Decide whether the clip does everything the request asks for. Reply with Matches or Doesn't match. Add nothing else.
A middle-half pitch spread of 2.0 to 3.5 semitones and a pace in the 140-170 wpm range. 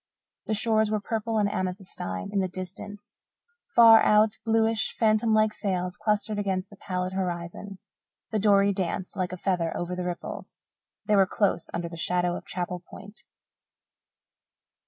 Matches